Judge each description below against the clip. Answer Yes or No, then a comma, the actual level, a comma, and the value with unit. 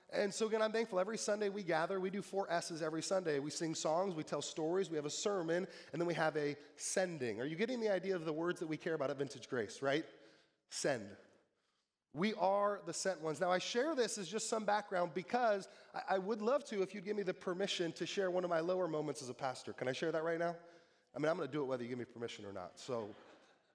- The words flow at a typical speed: No, fast, 265 wpm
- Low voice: No, medium, 175 Hz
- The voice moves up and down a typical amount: Yes, average, 4.3 semitones